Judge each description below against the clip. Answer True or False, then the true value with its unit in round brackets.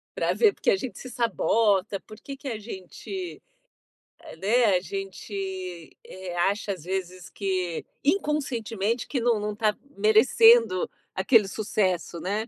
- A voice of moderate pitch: False (205 Hz)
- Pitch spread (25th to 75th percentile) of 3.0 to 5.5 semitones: True (3.7 semitones)